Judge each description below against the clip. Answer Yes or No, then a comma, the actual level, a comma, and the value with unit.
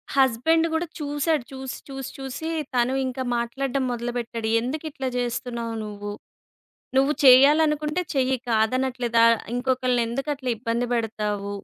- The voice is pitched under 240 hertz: No, very high, 255 Hz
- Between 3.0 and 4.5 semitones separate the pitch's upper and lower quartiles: No, narrow, 2.5 semitones